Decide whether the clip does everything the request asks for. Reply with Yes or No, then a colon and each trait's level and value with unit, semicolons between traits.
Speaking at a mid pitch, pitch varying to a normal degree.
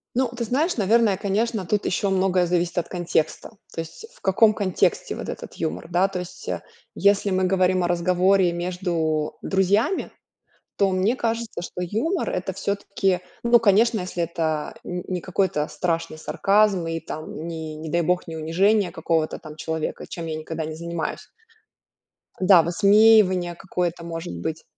Yes: medium, 180 Hz; average, 3.2 semitones